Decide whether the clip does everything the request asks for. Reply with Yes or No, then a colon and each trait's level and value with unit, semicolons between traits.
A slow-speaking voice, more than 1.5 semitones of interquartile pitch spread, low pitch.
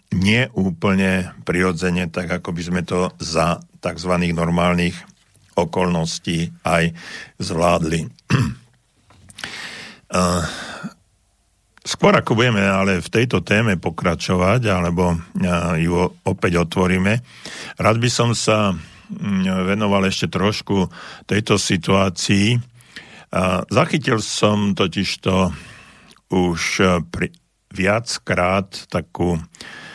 Yes: slow, 85 wpm; narrow, 2.5 semitones; very low, 90 Hz